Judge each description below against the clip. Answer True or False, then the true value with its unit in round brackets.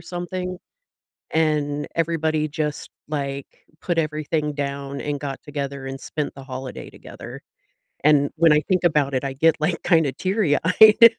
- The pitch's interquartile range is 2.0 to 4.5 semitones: True (2.9 semitones)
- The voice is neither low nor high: True (150 Hz)